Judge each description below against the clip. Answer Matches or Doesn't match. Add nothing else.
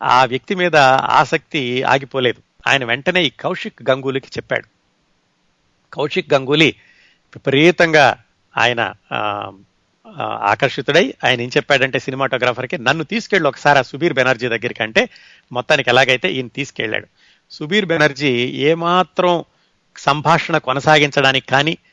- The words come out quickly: Doesn't match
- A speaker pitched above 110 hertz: Matches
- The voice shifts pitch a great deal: Doesn't match